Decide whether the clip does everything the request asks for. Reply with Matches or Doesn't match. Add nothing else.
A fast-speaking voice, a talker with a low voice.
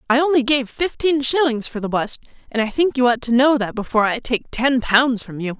Doesn't match